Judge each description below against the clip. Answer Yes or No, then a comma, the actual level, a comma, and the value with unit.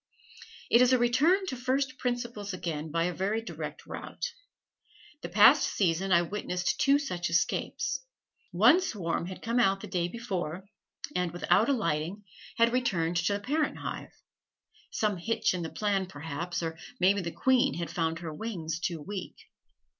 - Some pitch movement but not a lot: No, wide, 5.9 semitones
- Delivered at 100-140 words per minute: No, average, 165 wpm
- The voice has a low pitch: No, high, 195 Hz